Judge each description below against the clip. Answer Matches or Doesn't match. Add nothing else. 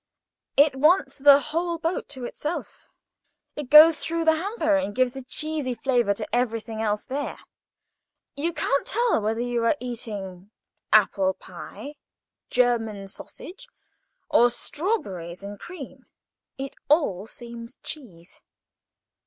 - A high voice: Matches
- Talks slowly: Matches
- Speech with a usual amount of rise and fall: Doesn't match